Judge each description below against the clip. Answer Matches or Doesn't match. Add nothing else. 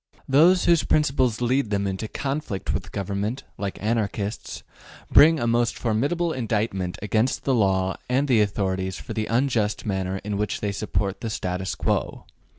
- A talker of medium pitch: Doesn't match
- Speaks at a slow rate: Doesn't match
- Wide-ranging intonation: Doesn't match